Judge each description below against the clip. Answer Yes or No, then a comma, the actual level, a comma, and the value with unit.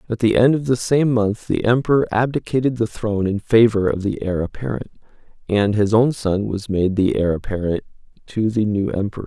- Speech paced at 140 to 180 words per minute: No, average, 200 wpm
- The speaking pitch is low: Yes, low, 110 Hz